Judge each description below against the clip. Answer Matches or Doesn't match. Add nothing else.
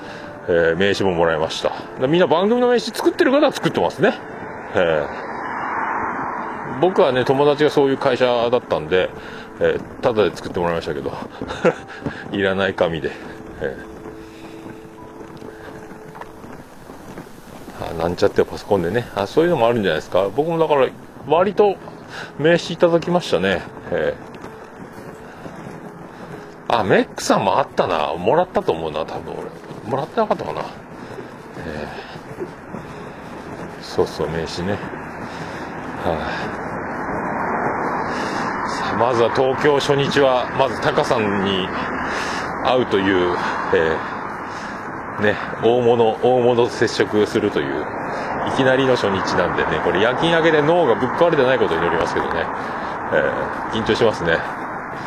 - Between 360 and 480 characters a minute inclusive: Doesn't match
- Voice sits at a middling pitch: Matches